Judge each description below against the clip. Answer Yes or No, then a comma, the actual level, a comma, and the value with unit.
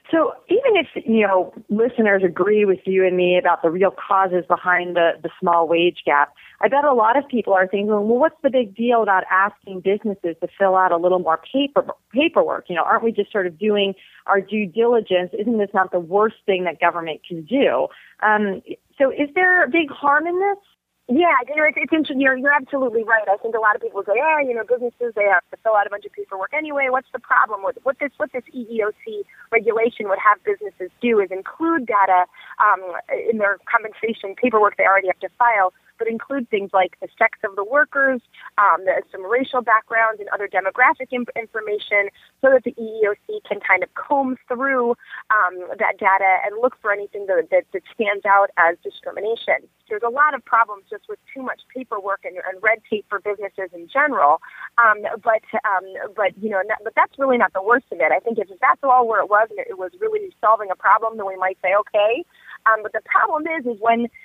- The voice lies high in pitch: Yes, high, 220 Hz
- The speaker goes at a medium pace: No, fast, 220 wpm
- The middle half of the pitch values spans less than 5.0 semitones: No, wide, 5.4 semitones